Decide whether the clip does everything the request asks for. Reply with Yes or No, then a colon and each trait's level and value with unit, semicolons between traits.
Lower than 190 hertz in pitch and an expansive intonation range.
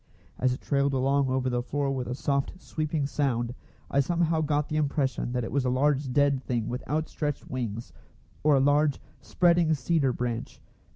No: medium, 140 Hz; average, 2.7 semitones